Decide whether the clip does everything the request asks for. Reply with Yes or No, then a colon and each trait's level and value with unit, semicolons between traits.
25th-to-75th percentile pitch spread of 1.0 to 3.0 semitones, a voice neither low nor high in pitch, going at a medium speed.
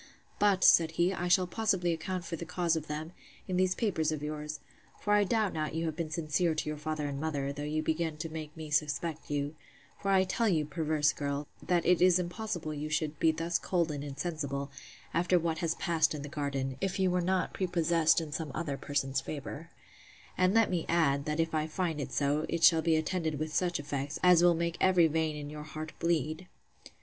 No: average, 2.7 semitones; medium, 160 Hz; fast, 220 wpm